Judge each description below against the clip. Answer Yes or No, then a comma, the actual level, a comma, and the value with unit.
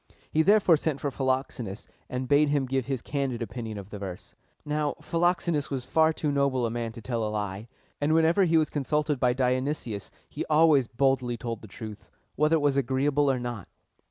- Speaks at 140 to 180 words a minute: No, average, 195 wpm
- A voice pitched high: No, low, 135 Hz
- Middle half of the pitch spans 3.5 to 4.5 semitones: Yes, average, 4.1 semitones